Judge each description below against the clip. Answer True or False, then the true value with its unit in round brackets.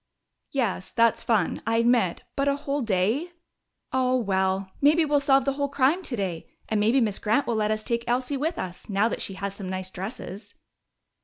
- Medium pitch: False (230 Hz)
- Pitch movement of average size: False (5.7 semitones)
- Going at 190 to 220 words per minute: True (200 wpm)